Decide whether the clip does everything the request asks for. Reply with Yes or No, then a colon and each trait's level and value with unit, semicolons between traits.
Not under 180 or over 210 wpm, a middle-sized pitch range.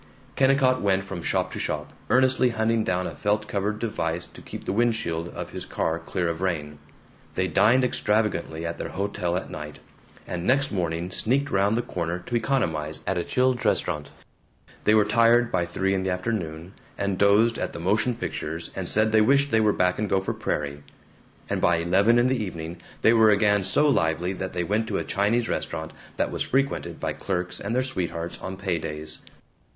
Yes: average, 195 wpm; average, 4.8 semitones